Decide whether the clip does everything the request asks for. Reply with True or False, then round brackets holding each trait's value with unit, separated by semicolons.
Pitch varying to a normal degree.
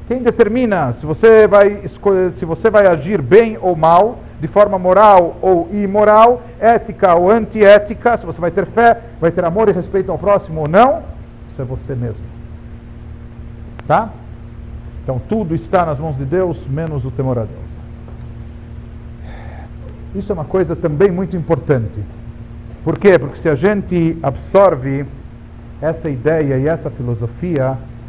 False (7.2 semitones)